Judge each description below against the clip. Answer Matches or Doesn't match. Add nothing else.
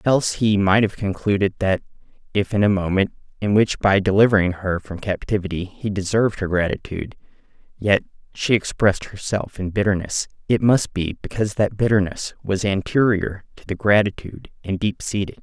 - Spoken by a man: Matches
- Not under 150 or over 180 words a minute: Matches